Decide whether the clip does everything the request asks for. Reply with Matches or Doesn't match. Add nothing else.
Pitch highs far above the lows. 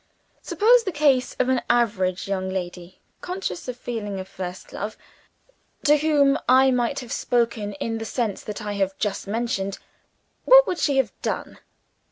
Matches